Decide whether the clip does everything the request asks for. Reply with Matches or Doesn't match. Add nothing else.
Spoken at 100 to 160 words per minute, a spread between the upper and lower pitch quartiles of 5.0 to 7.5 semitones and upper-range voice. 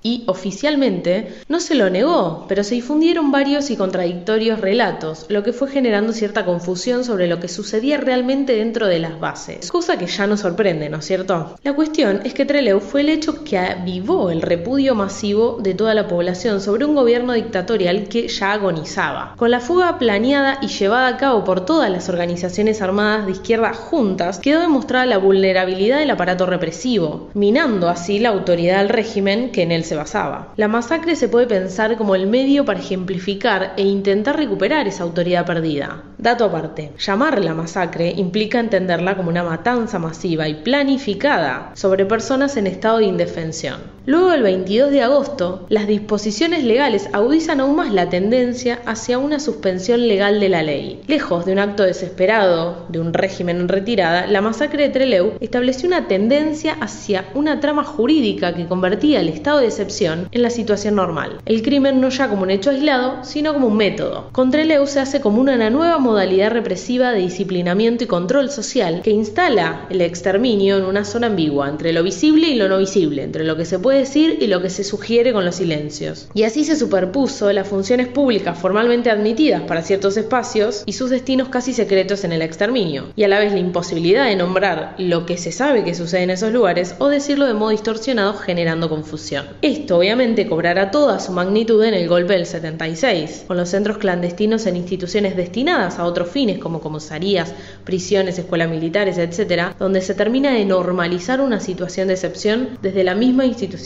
Doesn't match